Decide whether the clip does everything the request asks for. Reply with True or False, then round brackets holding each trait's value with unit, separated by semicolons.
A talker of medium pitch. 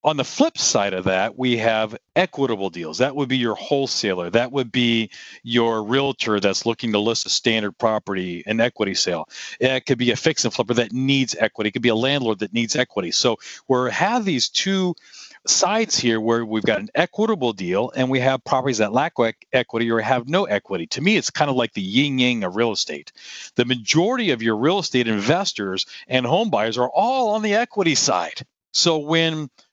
False (125 Hz)